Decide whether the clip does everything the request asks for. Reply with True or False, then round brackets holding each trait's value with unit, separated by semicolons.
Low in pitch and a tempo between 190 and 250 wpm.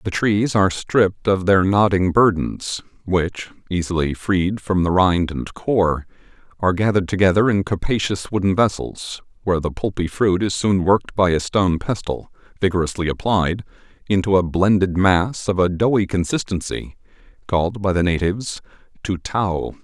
False (95 Hz; 150 wpm)